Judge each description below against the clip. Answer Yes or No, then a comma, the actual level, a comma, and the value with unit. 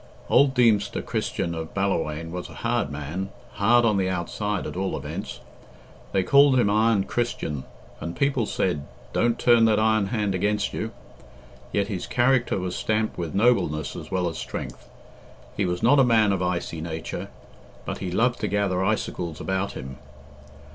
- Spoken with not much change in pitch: No, average, 4.2 semitones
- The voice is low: Yes, low, 100 Hz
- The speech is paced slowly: No, average, 170 wpm